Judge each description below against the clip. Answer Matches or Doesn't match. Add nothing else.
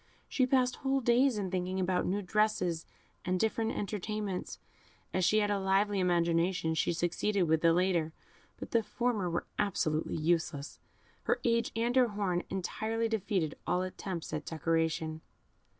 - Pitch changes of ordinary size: Matches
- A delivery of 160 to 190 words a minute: Doesn't match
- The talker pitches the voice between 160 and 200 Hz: Matches